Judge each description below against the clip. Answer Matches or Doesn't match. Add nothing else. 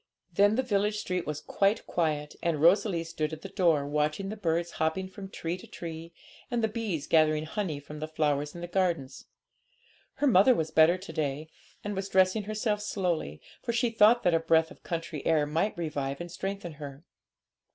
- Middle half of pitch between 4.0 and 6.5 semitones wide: Matches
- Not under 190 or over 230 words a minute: Matches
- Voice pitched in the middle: Matches